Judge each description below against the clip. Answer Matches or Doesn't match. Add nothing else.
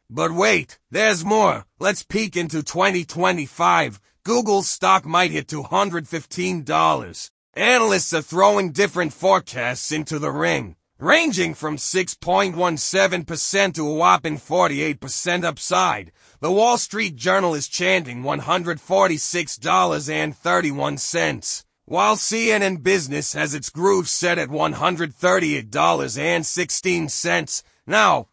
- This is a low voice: Doesn't match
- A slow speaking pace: Matches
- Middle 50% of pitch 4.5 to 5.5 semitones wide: Doesn't match